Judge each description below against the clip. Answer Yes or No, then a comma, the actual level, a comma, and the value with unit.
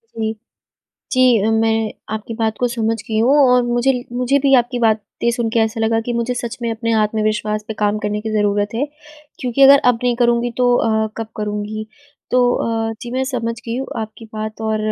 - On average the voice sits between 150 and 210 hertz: No, high, 225 Hz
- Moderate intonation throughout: No, narrow, 2.0 semitones